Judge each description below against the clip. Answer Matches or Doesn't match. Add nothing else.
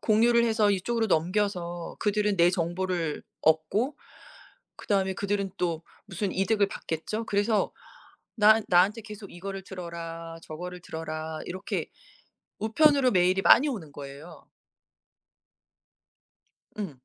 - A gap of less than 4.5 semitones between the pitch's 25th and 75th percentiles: Matches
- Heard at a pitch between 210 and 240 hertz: Doesn't match